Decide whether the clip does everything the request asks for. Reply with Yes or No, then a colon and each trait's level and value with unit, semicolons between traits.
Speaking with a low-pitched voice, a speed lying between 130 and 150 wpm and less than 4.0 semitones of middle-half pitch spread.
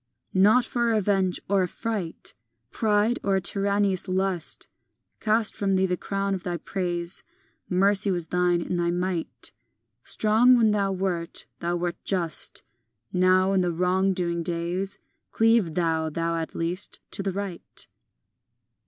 No: medium, 185 Hz; average, 145 wpm; narrow, 2.5 semitones